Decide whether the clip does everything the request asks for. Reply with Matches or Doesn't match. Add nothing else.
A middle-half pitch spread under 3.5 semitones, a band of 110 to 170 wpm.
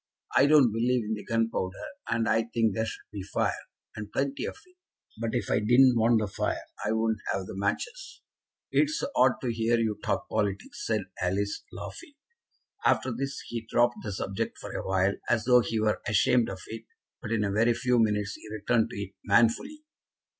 Doesn't match